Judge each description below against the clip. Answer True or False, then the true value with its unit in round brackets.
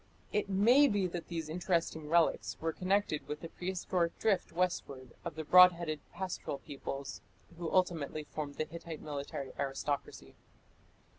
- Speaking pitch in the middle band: True (170 Hz)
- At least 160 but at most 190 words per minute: False (145 wpm)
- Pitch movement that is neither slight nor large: True (3.3 semitones)